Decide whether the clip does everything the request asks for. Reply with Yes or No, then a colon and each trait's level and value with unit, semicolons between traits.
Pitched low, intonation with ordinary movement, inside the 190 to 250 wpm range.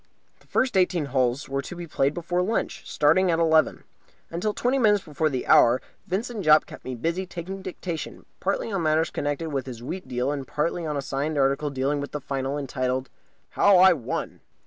No: medium, 155 Hz; average, 4.8 semitones; average, 195 wpm